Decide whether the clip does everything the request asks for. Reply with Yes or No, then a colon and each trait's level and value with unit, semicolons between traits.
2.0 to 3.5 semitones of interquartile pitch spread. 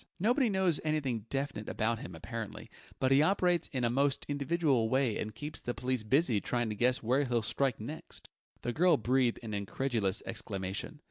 No: average, 4.6 semitones